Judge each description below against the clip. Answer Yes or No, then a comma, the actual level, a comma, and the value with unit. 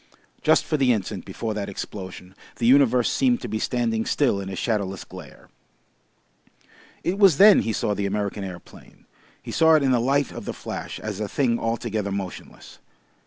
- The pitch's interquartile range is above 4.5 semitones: Yes, average, 5.1 semitones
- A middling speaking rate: Yes, average, 180 wpm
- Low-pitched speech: Yes, low, 110 Hz